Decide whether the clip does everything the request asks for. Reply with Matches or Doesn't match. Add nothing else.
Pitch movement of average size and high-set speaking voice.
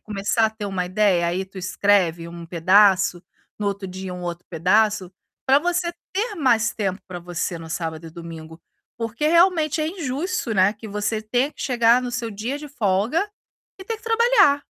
Doesn't match